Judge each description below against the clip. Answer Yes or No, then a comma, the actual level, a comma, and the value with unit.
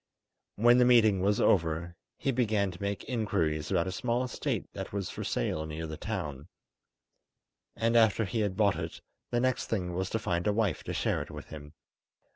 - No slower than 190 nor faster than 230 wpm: Yes, average, 195 wpm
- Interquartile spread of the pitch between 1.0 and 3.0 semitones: No, average, 5.0 semitones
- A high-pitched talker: No, low, 100 Hz